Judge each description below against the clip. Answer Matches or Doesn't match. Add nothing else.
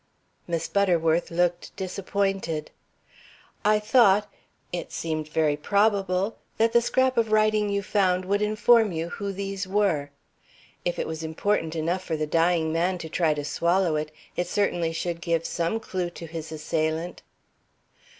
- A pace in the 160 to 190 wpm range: Doesn't match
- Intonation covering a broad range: Doesn't match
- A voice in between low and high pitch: Matches